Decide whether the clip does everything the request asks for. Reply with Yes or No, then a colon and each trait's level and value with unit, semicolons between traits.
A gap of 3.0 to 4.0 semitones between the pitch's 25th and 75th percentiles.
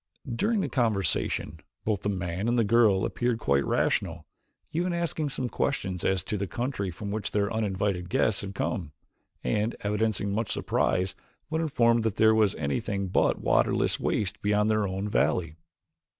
Yes: average, 3.5 semitones